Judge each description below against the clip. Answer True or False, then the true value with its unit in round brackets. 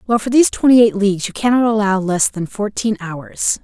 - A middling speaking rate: False (215 wpm)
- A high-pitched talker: True (210 Hz)